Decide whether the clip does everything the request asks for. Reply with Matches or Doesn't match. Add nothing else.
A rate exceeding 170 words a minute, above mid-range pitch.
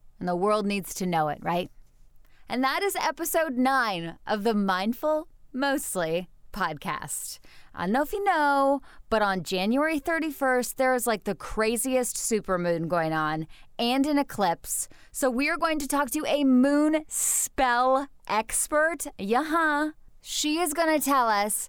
Doesn't match